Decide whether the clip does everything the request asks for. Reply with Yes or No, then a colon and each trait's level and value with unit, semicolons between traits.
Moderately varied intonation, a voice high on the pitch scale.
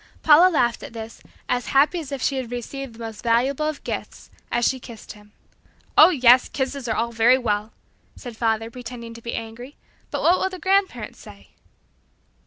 Yes: average, 3.4 semitones; high, 245 Hz